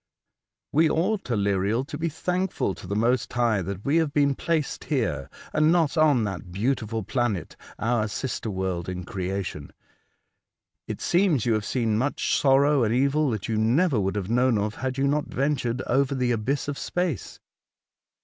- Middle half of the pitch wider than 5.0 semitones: Yes, wide, 5.6 semitones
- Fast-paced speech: No, average, 175 wpm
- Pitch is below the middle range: Yes, low, 125 Hz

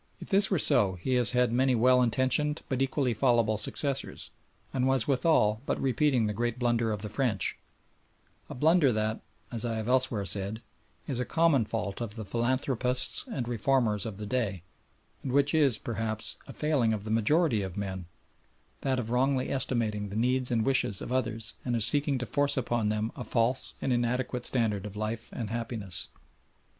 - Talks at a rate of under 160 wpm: No, average, 185 wpm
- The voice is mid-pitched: No, low, 120 Hz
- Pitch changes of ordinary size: Yes, average, 3.2 semitones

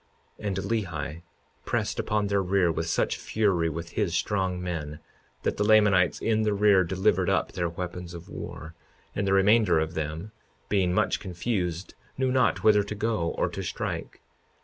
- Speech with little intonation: No, average, 3.5 semitones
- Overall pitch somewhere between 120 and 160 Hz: No, very low, 95 Hz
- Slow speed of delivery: No, average, 170 wpm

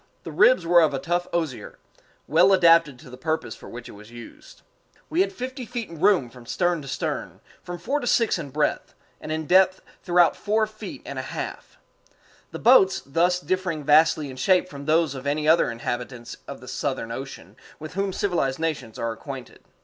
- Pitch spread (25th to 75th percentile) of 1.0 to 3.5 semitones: No, wide, 5.6 semitones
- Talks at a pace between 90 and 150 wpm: No, average, 195 wpm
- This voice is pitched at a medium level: Yes, medium, 160 Hz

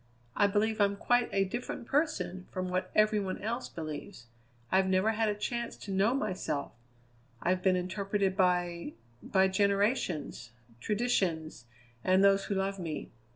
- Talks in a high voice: Yes, high, 195 Hz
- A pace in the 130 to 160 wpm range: Yes, average, 150 wpm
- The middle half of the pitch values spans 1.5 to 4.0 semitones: Yes, narrow, 2.6 semitones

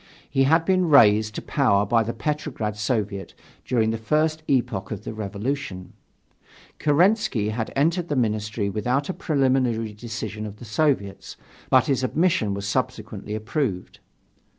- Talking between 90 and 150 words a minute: Yes, average, 145 wpm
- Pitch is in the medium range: No, low, 115 Hz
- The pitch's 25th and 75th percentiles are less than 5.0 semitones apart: No, wide, 5.4 semitones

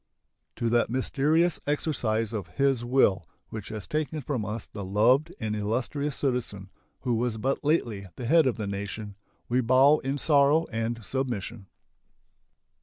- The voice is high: No, low, 120 Hz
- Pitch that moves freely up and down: No, average, 4.6 semitones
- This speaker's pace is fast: No, average, 150 wpm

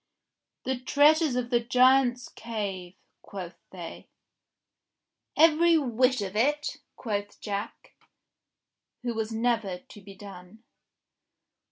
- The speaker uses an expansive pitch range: No, average, 4.3 semitones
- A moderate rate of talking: No, slow, 100 wpm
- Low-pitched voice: No, high, 230 Hz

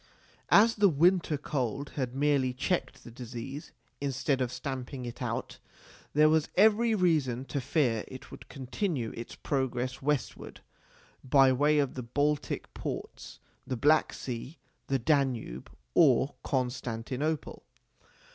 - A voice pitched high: No, low, 135 Hz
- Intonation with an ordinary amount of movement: Yes, average, 3.2 semitones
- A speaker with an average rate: No, slow, 130 wpm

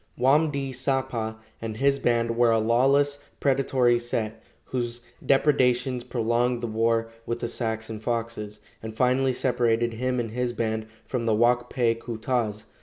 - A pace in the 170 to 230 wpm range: No, average, 160 wpm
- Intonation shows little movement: Yes, narrow, 2.1 semitones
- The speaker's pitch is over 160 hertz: No, low, 120 Hz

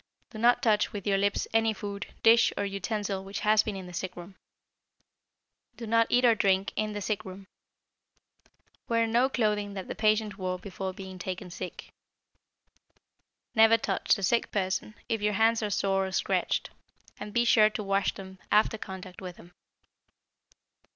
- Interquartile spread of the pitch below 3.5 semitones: Yes, narrow, 2.5 semitones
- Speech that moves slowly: No, average, 170 wpm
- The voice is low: No, high, 205 Hz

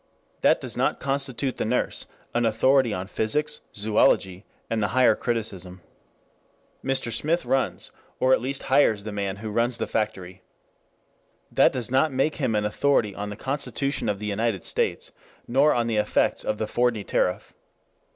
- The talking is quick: No, average, 165 wpm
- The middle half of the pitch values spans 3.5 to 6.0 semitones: Yes, average, 4.1 semitones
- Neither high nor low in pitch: No, low, 115 Hz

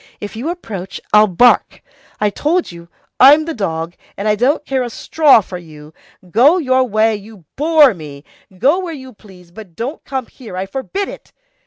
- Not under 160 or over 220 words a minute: Yes, average, 185 wpm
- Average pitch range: No, wide, 6.9 semitones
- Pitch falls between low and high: No, high, 225 Hz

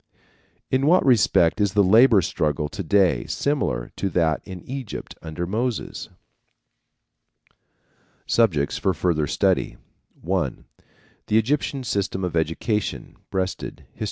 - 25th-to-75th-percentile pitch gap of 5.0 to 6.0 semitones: Yes, wide, 5.6 semitones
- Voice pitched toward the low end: Yes, very low, 95 Hz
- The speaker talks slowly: Yes, slow, 125 wpm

